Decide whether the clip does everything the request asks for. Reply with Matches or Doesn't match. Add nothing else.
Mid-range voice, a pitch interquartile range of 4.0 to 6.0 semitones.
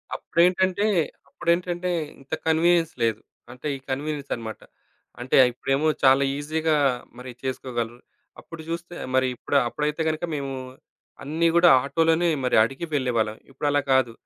Matches